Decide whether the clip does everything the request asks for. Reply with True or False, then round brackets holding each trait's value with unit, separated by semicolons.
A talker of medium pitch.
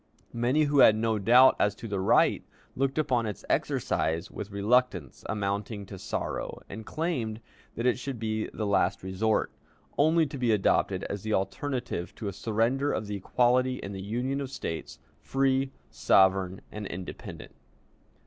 False (110 Hz)